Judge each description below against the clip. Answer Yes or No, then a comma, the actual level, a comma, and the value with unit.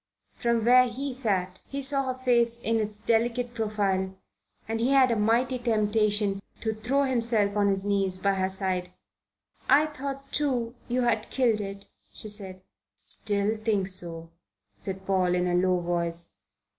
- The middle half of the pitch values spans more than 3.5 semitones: Yes, average, 4.0 semitones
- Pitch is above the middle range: Yes, high, 215 Hz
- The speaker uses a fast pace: No, average, 160 wpm